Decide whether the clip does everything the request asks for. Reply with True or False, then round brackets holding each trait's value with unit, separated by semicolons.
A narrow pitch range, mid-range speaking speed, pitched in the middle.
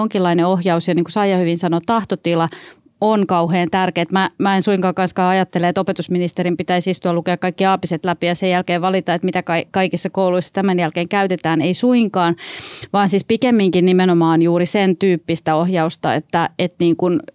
False (1.8 semitones; 175 wpm; 180 Hz)